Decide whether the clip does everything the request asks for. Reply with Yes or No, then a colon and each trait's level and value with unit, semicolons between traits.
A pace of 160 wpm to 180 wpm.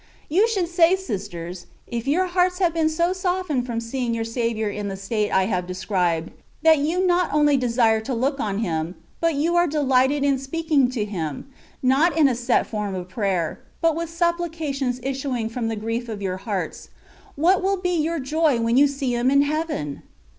No: average, 195 wpm